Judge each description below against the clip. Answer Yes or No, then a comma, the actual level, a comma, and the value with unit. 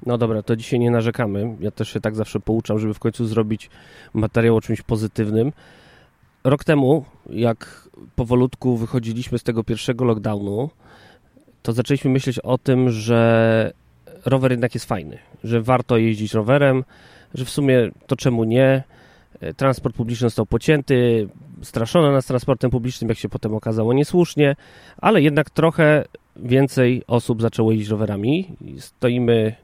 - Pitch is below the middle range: Yes, low, 120 Hz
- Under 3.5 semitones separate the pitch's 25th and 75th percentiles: Yes, average, 2.9 semitones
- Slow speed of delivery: No, average, 145 wpm